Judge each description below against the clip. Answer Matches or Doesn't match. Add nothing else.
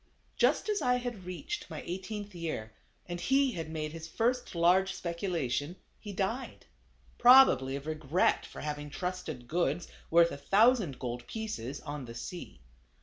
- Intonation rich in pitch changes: Matches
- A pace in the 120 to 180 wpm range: Matches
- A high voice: Doesn't match